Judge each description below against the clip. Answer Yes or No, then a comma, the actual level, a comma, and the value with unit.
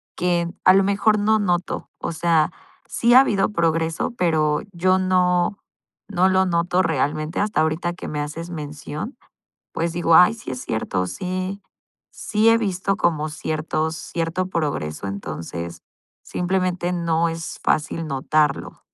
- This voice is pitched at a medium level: Yes, medium, 170 Hz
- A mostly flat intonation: No, average, 3.3 semitones